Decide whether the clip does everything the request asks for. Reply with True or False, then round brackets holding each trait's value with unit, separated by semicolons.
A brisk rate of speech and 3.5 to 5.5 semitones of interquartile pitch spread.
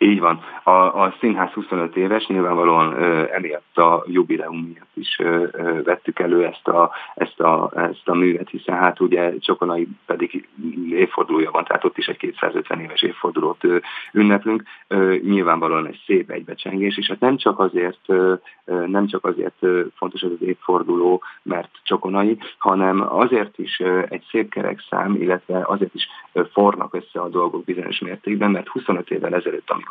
True (165 wpm; 3.8 semitones)